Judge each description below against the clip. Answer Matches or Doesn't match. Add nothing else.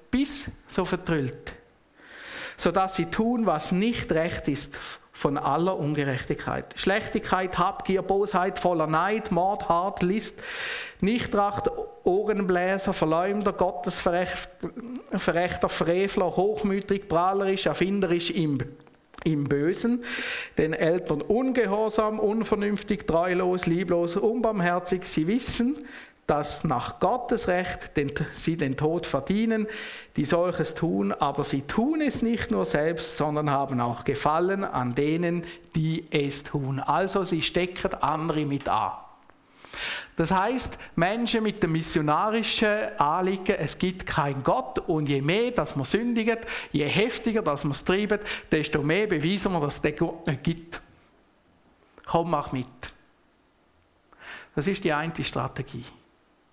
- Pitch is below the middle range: Doesn't match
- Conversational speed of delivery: Doesn't match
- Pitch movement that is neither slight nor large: Matches